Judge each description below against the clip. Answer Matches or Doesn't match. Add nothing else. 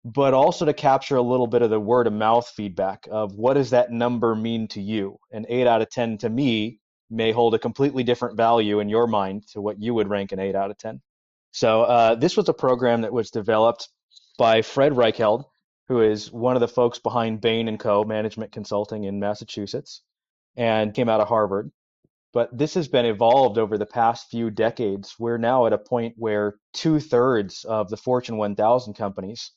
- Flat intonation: Matches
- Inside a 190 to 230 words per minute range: Matches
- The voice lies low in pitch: Matches